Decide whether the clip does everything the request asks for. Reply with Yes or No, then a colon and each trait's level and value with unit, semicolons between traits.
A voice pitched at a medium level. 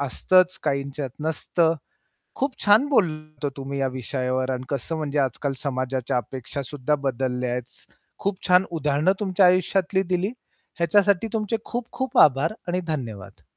Yes: medium, 150 Hz